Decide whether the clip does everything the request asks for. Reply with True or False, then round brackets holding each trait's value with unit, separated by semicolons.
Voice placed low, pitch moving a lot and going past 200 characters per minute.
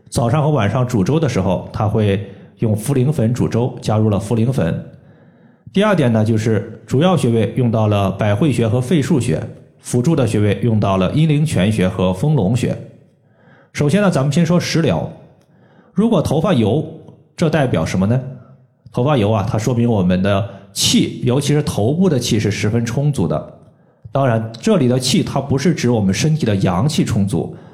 True (125 Hz; 5.7 semitones; 265 characters per minute)